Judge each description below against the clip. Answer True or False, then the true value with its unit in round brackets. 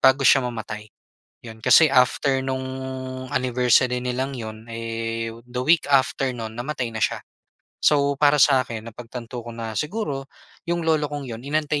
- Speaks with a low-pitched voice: True (125 Hz)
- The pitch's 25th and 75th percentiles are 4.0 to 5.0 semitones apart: False (3.6 semitones)